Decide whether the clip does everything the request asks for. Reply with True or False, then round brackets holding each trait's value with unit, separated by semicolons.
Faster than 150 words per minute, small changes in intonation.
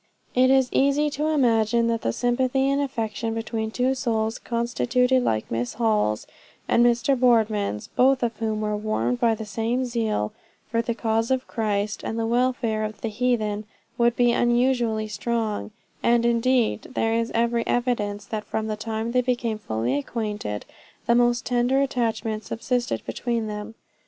True (160 wpm; 2.3 semitones)